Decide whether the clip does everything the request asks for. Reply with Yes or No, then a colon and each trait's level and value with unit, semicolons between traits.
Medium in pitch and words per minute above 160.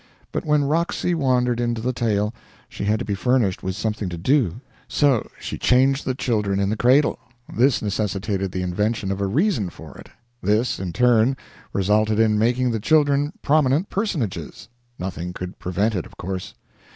No: low, 110 Hz; average, 175 wpm